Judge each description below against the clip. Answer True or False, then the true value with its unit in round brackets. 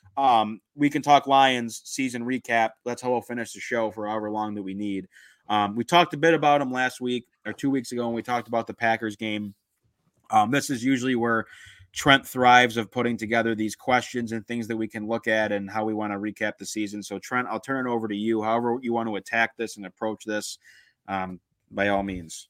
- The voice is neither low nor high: False (115 Hz)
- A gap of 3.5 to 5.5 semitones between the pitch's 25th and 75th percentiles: False (2.8 semitones)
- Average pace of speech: False (230 wpm)